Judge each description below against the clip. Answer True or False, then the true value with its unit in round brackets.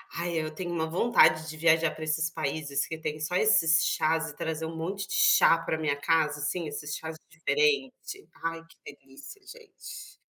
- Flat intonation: True (2.1 semitones)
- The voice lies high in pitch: False (160 Hz)